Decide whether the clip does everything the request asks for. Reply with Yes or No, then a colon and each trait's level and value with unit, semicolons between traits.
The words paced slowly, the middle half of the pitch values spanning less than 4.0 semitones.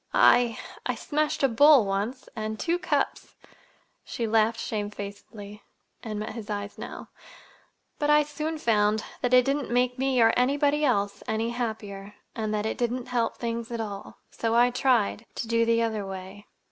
No: average, 155 wpm; average, 3.0 semitones